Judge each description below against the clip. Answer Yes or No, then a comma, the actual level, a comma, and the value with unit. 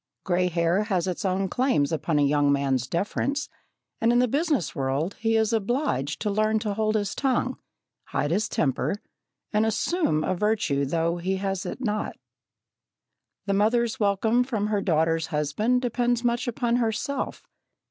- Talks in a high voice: Yes, high, 205 Hz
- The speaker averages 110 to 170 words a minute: Yes, average, 160 wpm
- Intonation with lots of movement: Yes, wide, 6.0 semitones